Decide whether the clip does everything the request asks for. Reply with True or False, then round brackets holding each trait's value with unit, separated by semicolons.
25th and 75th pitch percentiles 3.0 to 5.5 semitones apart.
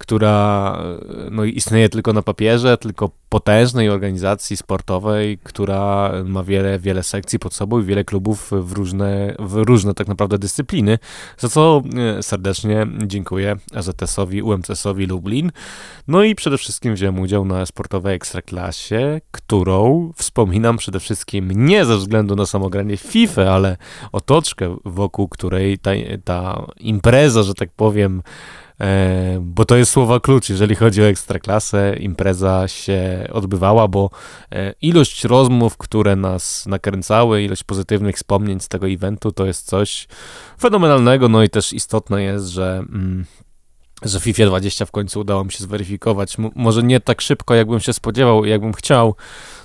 False (2.5 semitones)